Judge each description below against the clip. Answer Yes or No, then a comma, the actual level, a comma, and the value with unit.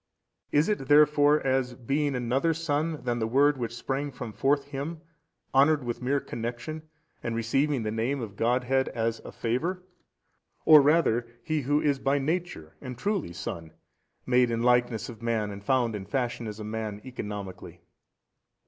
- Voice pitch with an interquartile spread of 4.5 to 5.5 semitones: No, average, 4.1 semitones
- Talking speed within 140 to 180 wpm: Yes, average, 165 wpm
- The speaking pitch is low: Yes, low, 125 Hz